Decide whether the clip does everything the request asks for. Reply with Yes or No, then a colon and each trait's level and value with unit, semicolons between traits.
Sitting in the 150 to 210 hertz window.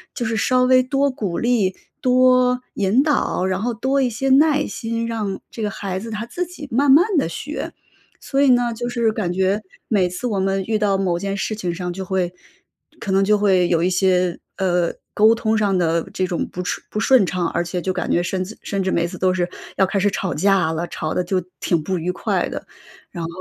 Yes: high, 200 Hz